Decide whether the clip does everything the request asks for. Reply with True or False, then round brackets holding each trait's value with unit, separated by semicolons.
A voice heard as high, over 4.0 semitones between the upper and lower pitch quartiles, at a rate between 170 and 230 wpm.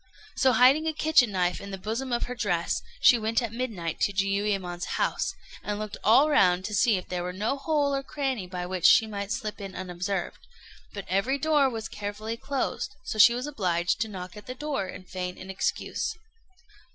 True (210 Hz; 5.3 semitones; 200 wpm)